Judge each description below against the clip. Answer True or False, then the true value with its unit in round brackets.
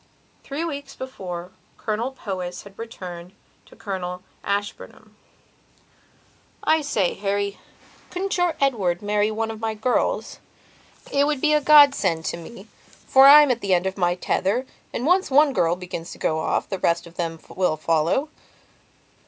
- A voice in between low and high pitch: False (205 Hz)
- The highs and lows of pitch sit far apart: True (7.3 semitones)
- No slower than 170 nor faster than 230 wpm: False (160 wpm)